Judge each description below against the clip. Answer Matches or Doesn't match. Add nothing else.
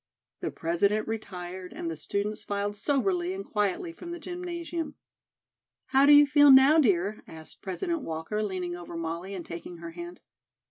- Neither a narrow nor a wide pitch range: Doesn't match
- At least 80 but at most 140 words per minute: Doesn't match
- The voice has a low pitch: Doesn't match